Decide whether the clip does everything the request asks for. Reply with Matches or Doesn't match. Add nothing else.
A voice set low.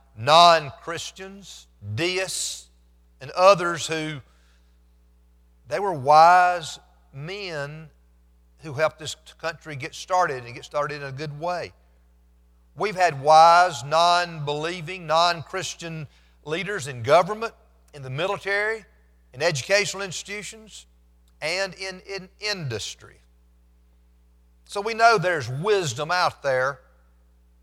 Doesn't match